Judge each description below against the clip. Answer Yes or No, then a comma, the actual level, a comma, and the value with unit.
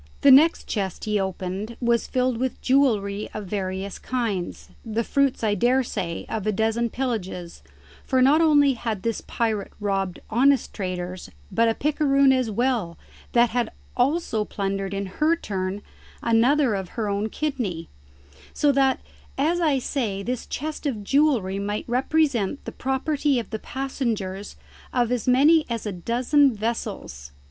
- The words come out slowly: No, average, 150 wpm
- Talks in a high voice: Yes, high, 230 Hz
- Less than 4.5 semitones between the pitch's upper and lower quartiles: No, average, 5.1 semitones